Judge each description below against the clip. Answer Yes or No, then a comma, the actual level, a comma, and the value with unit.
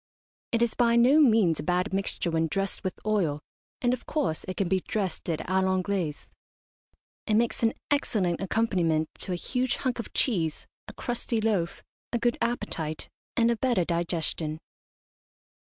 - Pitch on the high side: Yes, high, 195 Hz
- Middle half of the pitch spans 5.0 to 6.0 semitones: Yes, wide, 5.5 semitones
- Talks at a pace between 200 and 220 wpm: No, average, 165 wpm